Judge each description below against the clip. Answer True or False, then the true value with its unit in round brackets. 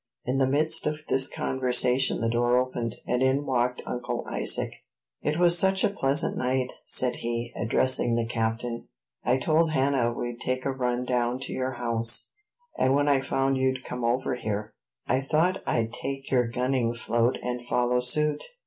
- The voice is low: True (125 Hz)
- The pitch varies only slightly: True (1.9 semitones)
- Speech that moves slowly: False (175 wpm)